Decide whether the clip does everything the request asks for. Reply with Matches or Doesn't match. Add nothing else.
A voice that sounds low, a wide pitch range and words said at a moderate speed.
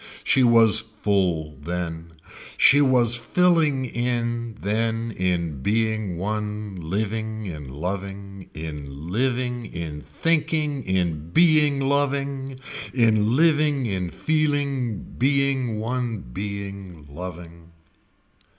Doesn't match